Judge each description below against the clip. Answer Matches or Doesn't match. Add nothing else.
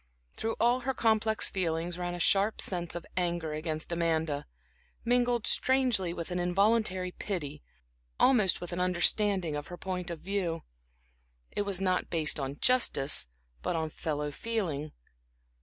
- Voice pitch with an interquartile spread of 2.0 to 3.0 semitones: Doesn't match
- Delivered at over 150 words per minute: Doesn't match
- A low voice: Doesn't match